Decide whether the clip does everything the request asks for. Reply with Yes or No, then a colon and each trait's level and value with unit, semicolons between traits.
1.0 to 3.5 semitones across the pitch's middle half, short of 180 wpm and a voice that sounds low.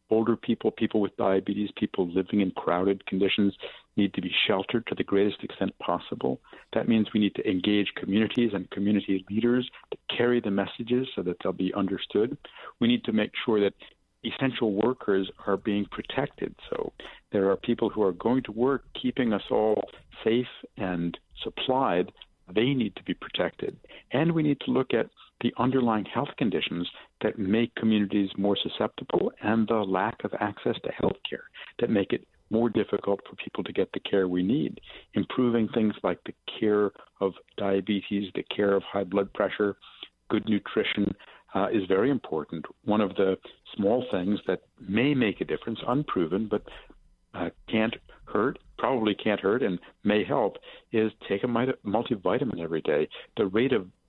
Yes: average, 2.9 semitones; average, 170 wpm; low, 105 Hz